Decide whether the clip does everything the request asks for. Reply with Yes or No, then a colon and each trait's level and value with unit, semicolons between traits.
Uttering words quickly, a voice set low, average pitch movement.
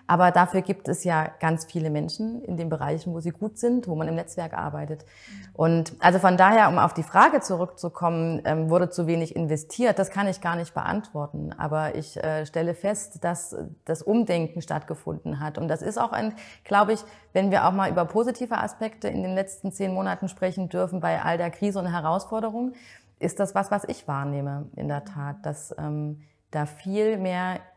No: fast, 195 wpm; medium, 175 Hz; average, 3.9 semitones